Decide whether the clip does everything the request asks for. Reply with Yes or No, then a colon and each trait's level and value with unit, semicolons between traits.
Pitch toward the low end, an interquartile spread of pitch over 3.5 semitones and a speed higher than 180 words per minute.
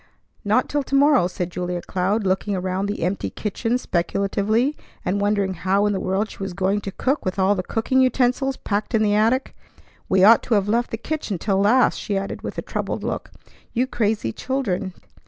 No: high, 205 Hz; average, 3.9 semitones; average, 200 wpm